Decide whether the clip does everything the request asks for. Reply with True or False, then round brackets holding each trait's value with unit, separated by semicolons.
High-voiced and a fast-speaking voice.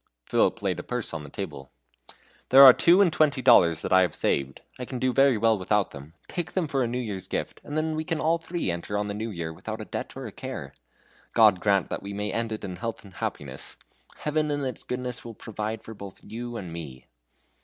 False (110 Hz; 240 wpm)